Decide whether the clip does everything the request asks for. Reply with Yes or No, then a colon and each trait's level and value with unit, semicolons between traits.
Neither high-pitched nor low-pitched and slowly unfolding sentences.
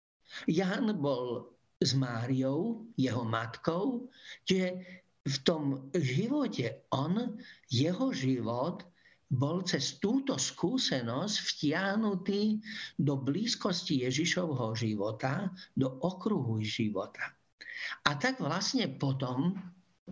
Yes: medium, 165 Hz; slow, 85 wpm